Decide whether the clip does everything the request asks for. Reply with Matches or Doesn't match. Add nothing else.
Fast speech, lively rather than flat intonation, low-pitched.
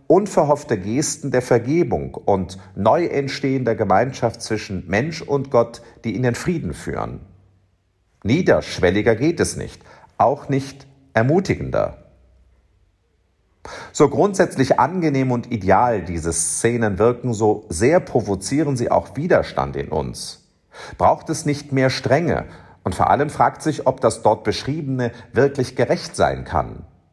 Doesn't match